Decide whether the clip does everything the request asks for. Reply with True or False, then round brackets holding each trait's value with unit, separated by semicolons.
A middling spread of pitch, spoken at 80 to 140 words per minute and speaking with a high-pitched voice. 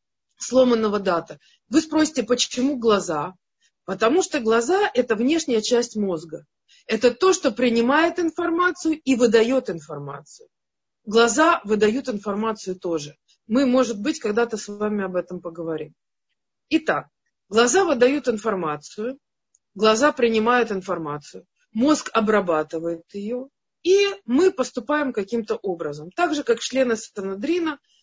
False (6.3 semitones; 115 wpm; 235 Hz)